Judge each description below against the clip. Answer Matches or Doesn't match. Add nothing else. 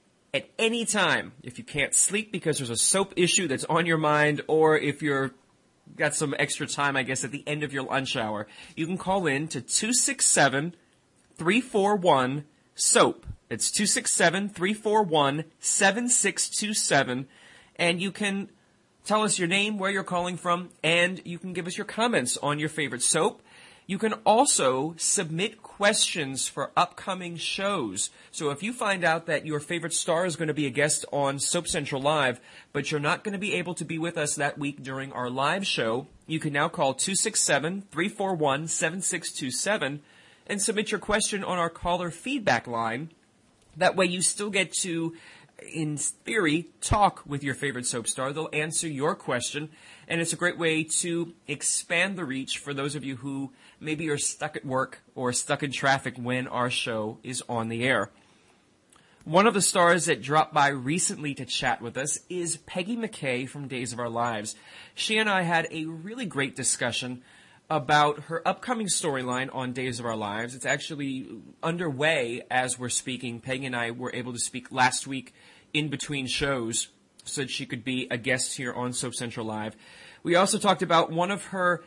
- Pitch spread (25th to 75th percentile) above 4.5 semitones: Matches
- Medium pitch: Matches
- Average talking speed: Matches